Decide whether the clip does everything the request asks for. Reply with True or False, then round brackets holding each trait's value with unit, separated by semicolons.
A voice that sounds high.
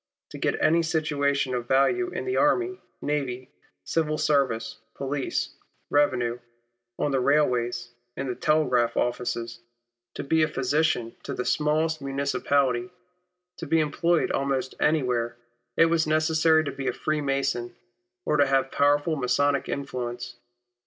False (140 Hz)